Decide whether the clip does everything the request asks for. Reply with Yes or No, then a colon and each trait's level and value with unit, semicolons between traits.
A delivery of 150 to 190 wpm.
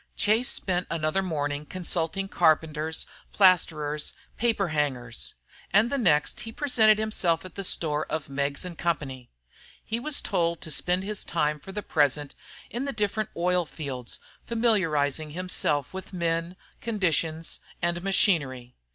No: average, 140 wpm